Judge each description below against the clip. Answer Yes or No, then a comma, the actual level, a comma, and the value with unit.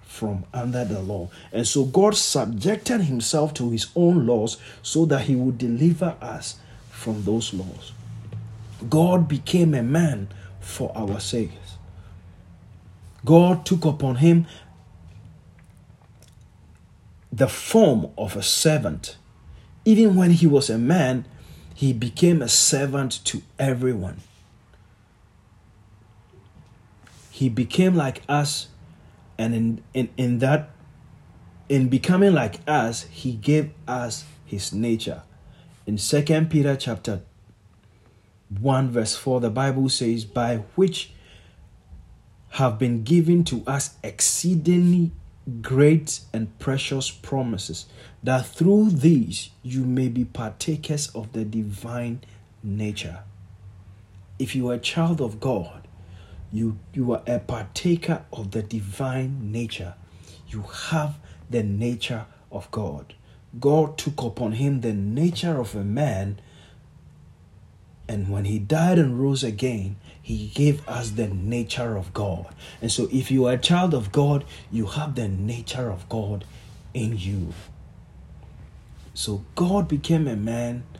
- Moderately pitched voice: No, low, 115 Hz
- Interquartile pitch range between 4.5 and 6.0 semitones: Yes, wide, 5.4 semitones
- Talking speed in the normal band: No, slow, 125 wpm